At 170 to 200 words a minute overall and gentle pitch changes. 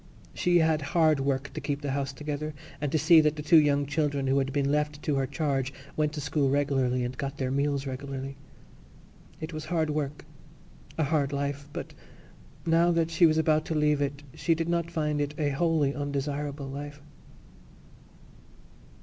Yes: average, 175 wpm; narrow, 1.9 semitones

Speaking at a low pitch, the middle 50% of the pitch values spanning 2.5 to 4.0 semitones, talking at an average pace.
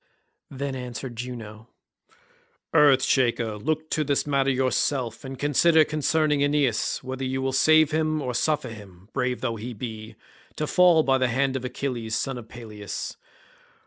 Yes: low, 130 Hz; average, 3.6 semitones; average, 155 wpm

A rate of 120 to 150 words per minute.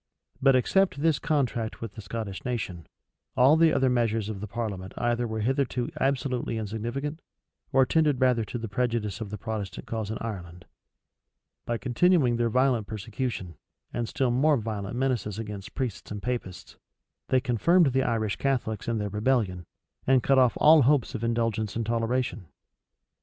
No: average, 165 wpm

